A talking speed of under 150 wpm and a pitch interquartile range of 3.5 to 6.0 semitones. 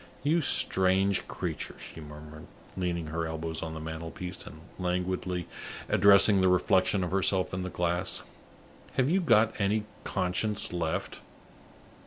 No: slow, 135 wpm; average, 3.1 semitones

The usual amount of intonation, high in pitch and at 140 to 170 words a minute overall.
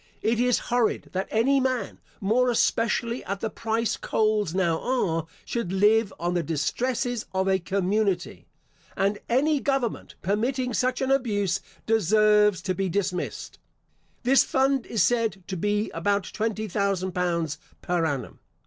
Yes: average, 4.2 semitones; high, 210 Hz; average, 145 wpm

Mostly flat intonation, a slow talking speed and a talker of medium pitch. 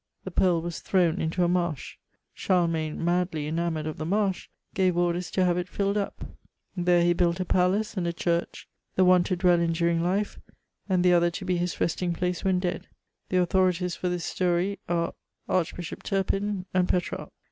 No: narrow, 1.3 semitones; average, 190 wpm; medium, 180 Hz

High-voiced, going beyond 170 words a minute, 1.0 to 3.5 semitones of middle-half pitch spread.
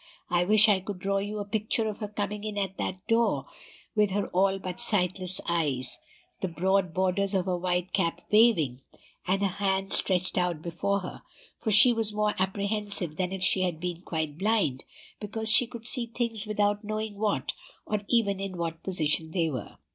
Yes: high, 195 Hz; average, 190 wpm; average, 2.8 semitones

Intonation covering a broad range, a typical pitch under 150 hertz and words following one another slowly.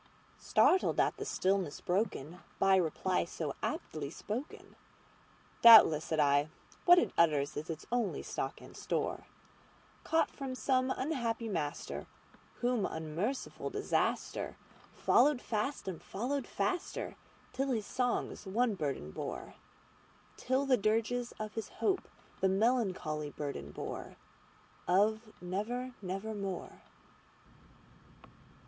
No: wide, 6.8 semitones; high, 210 Hz; slow, 100 wpm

